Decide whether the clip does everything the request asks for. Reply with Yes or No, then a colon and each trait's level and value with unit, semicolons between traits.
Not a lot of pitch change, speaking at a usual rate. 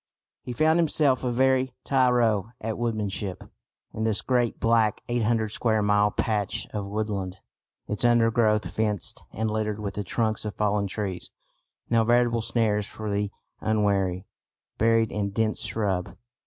Yes: narrow, 2.2 semitones; average, 145 wpm